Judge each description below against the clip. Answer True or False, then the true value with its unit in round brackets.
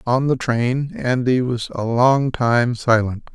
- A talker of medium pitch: False (125 Hz)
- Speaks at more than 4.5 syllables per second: False (3.6 syllables/s)